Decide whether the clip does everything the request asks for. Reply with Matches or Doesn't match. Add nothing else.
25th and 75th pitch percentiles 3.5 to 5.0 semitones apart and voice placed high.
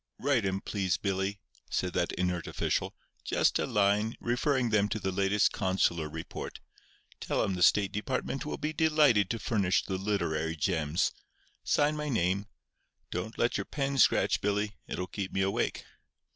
Doesn't match